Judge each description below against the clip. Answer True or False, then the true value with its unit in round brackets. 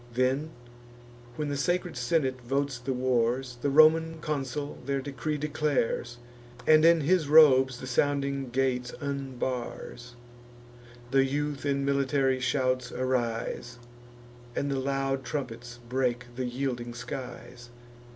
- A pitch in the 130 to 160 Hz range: True (135 Hz)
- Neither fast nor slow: False (120 wpm)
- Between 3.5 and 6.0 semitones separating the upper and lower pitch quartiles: False (2.4 semitones)